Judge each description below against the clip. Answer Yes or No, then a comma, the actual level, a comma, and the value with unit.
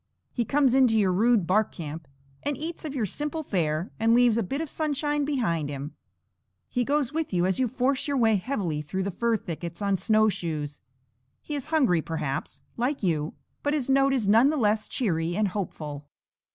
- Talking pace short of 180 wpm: No, average, 190 wpm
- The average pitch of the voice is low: No, high, 220 Hz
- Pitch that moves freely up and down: Yes, wide, 7.8 semitones